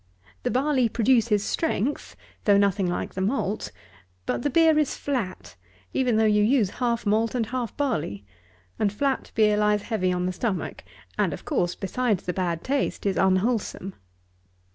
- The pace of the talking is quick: No, average, 165 wpm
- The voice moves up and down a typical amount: Yes, average, 4.8 semitones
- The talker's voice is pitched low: No, high, 215 Hz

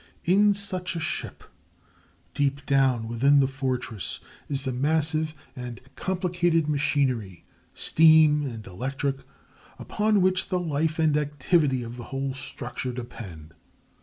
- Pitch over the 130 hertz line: Yes, medium, 140 Hz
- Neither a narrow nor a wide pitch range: Yes, average, 4.2 semitones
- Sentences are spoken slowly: Yes, slow, 125 wpm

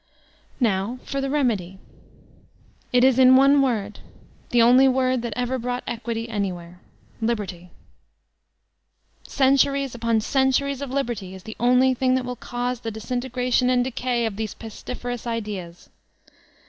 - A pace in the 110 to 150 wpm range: Yes, average, 145 wpm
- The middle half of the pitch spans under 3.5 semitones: Yes, average, 2.8 semitones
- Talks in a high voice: Yes, high, 245 Hz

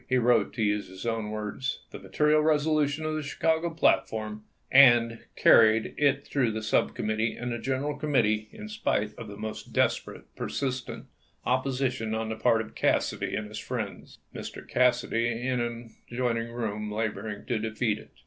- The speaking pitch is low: Yes, low, 120 Hz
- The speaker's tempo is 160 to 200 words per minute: Yes, average, 180 wpm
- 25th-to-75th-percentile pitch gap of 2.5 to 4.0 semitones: Yes, average, 3.6 semitones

